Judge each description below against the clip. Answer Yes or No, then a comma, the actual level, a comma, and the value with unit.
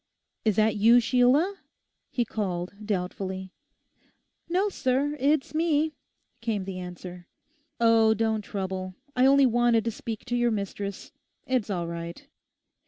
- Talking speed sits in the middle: No, slow, 130 wpm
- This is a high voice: Yes, high, 220 Hz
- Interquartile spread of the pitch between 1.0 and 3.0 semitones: No, average, 5.0 semitones